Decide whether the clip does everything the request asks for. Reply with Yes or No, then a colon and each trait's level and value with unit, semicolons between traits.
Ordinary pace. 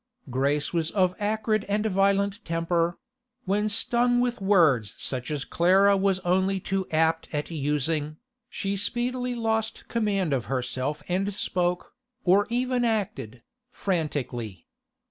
No: slow, 125 wpm